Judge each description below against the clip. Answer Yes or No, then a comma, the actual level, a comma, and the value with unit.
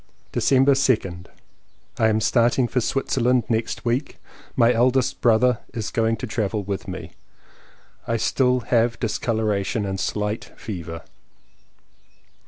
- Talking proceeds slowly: Yes, slow, 120 wpm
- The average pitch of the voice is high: No, low, 115 Hz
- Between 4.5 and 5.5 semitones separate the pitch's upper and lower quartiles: No, average, 3.0 semitones